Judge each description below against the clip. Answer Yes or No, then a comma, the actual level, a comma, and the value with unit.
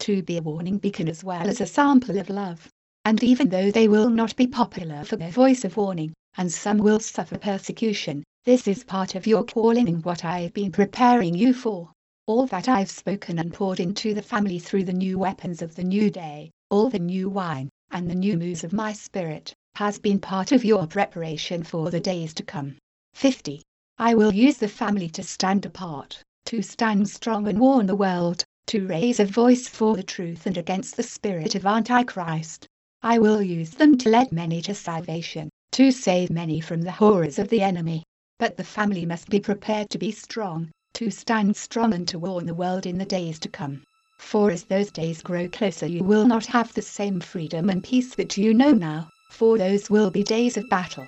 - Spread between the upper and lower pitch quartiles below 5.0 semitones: Yes, average, 3.9 semitones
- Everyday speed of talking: No, fast, 210 wpm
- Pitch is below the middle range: No, high, 200 Hz